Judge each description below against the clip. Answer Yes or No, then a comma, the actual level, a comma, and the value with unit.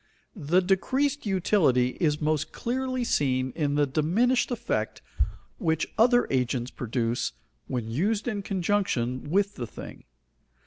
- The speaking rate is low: Yes, slow, 125 wpm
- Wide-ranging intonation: Yes, wide, 8.6 semitones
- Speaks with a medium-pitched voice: Yes, medium, 165 Hz